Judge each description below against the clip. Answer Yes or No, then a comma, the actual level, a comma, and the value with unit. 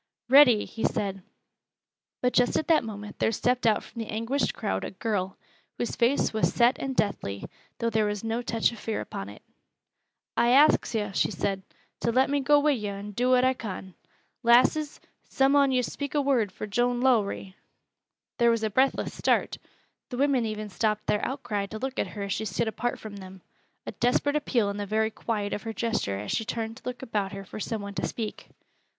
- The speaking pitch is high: Yes, high, 225 Hz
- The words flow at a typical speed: No, fast, 210 wpm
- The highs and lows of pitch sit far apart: No, average, 3.5 semitones